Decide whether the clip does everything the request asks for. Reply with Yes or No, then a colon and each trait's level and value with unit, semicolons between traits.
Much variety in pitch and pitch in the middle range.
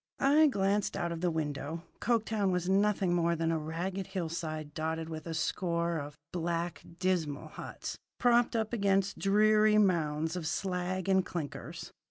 No: average, 3.3 semitones; medium, 175 Hz